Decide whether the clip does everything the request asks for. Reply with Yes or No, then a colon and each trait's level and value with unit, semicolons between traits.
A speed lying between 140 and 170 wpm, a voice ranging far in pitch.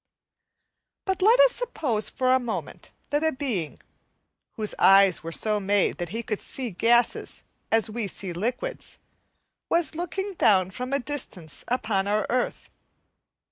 Yes: average, 145 wpm; wide, 6.4 semitones